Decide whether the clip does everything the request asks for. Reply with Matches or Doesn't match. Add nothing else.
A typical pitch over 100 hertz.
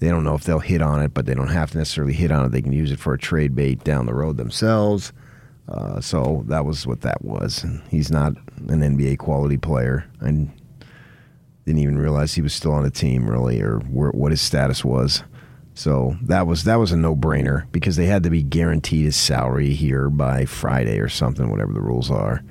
Doesn't match